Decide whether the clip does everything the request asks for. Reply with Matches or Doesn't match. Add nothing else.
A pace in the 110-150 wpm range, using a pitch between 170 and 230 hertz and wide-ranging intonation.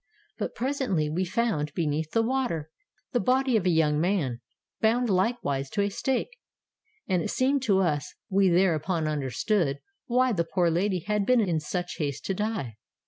Doesn't match